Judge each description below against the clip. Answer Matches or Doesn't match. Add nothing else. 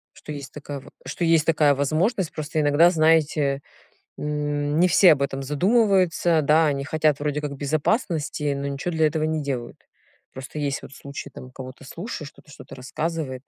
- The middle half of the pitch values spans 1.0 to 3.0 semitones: Matches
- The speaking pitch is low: Doesn't match